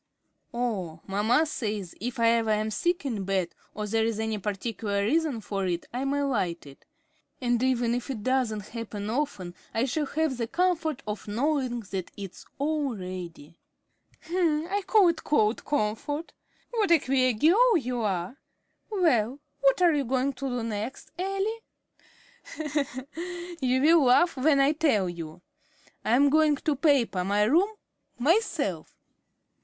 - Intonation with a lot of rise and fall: Yes, wide, 6.2 semitones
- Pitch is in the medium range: No, high, 245 Hz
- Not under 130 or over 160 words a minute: Yes, average, 150 wpm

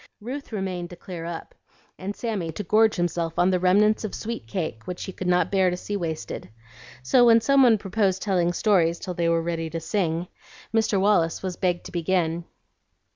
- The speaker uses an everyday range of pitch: Yes, average, 3.5 semitones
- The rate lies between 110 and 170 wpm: No, average, 195 wpm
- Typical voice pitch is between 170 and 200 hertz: Yes, medium, 185 Hz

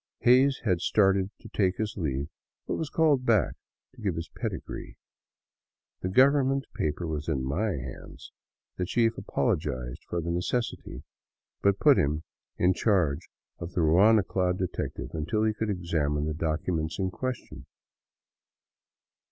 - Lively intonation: Yes, wide, 5.9 semitones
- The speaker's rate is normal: Yes, average, 145 wpm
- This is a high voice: No, very low, 90 Hz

